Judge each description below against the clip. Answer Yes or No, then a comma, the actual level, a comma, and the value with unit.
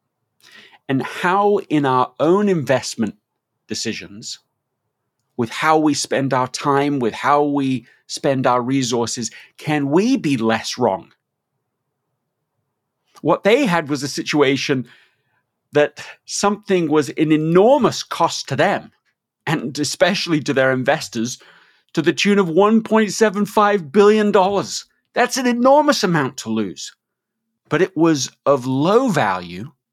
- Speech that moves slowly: Yes, slow, 120 wpm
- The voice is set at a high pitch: No, medium, 145 Hz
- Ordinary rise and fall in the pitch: No, wide, 7.1 semitones